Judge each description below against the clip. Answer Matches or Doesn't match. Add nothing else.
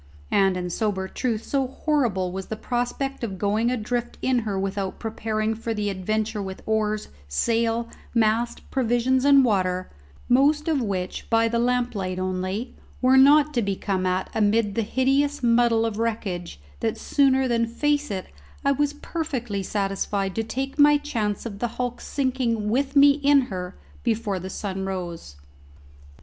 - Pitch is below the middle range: Doesn't match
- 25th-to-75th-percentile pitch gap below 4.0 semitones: Doesn't match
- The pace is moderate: Matches